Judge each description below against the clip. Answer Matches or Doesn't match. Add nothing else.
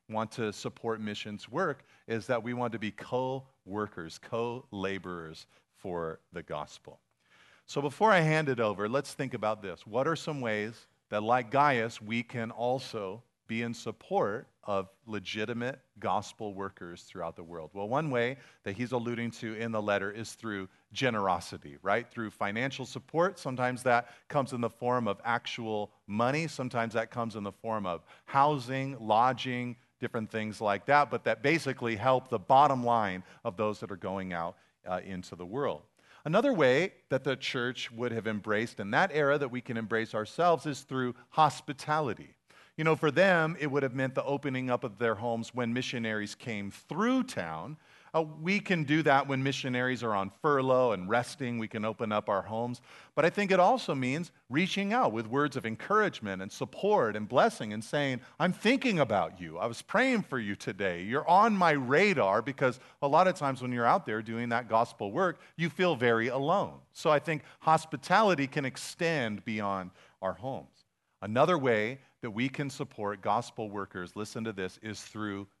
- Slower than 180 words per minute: Doesn't match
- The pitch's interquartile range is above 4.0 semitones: Matches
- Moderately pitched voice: Doesn't match